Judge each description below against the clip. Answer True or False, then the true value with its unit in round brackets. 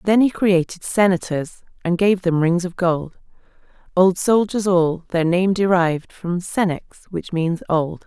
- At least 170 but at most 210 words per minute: False (155 wpm)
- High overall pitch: False (180 Hz)